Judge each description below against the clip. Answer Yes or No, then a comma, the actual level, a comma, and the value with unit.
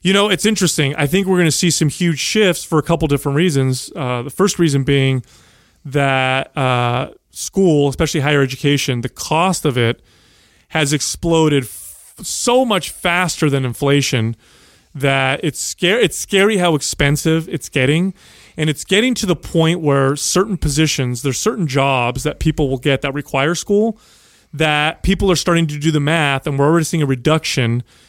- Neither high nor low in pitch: Yes, medium, 150 Hz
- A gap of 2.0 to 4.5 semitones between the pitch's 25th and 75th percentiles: Yes, average, 4.1 semitones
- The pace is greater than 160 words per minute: Yes, average, 175 wpm